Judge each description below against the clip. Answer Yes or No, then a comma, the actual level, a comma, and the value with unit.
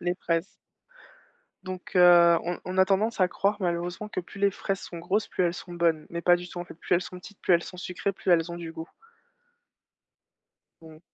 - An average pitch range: No, narrow, 1.7 semitones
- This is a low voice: No, medium, 175 Hz